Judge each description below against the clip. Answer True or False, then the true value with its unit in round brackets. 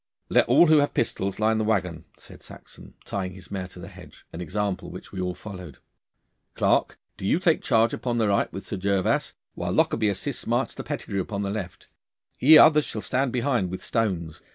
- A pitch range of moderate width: True (3.7 semitones)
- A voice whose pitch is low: True (100 Hz)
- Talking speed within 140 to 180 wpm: False (200 wpm)